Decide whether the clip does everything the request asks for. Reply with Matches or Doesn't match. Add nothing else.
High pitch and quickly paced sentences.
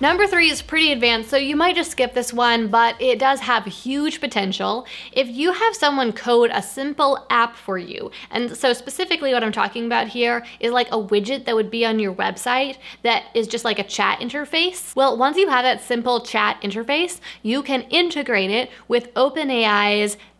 Doesn't match